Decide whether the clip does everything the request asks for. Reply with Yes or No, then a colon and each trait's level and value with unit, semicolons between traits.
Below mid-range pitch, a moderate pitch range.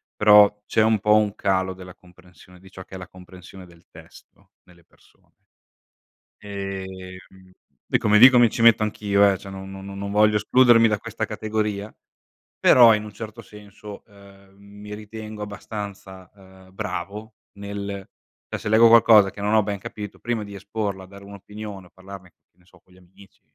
No: low, 100 Hz; narrow, 2.0 semitones